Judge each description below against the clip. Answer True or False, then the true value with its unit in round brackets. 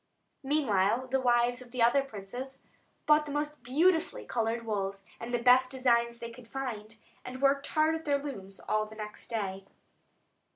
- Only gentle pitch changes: False (3.7 semitones)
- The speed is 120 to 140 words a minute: False (170 wpm)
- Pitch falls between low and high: False (245 Hz)